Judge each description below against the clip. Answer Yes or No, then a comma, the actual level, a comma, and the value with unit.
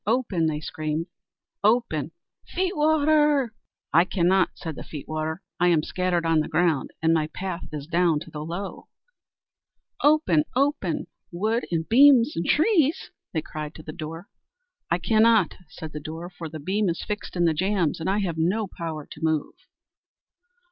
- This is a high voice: No, medium, 175 Hz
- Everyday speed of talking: Yes, average, 170 wpm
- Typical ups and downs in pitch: No, wide, 5.7 semitones